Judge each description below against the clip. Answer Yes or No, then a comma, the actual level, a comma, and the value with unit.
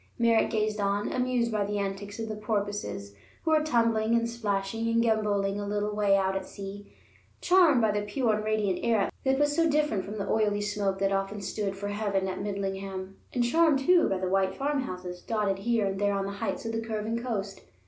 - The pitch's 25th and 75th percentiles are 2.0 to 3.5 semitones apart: Yes, average, 2.7 semitones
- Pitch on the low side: No, high, 210 Hz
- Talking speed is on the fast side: Yes, fast, 210 wpm